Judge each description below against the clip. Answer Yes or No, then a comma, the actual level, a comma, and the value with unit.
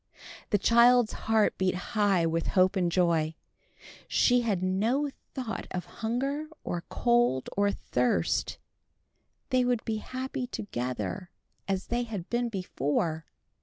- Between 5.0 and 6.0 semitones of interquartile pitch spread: Yes, average, 5.3 semitones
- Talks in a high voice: Yes, high, 205 Hz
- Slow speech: Yes, slow, 130 wpm